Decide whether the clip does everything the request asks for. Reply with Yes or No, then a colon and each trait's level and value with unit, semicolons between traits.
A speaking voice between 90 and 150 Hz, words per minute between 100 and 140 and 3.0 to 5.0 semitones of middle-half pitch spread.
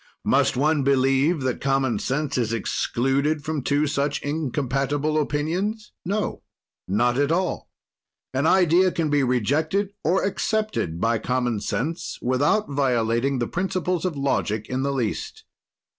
Yes: medium, 140 Hz; slow, 135 wpm; average, 4.0 semitones